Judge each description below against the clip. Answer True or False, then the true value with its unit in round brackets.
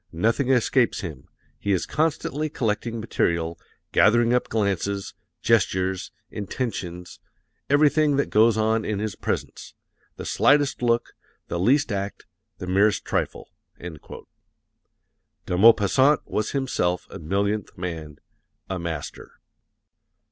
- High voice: False (105 Hz)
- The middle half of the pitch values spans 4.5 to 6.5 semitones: True (5.1 semitones)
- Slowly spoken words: True (110 wpm)